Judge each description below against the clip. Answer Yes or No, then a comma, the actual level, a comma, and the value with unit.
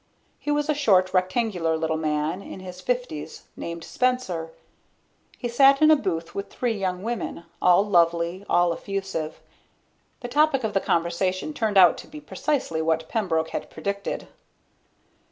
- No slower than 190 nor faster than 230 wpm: No, average, 155 wpm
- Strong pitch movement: Yes, wide, 6.3 semitones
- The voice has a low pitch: No, medium, 185 Hz